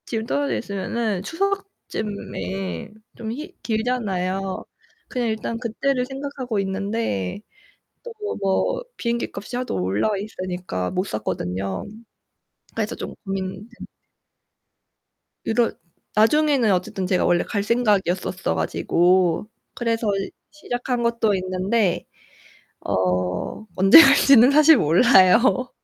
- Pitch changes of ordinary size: Yes, average, 5.0 semitones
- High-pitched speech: Yes, high, 215 Hz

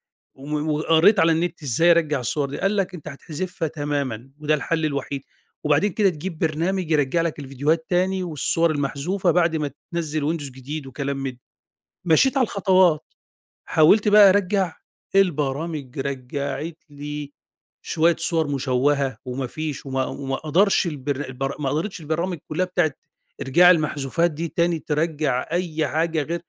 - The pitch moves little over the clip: No, average, 3.4 semitones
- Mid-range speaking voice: Yes, medium, 155 Hz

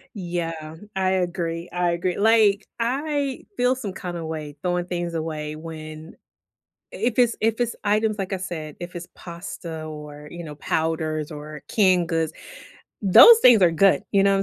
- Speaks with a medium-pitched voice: Yes, medium, 175 Hz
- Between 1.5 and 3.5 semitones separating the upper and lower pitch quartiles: No, average, 3.9 semitones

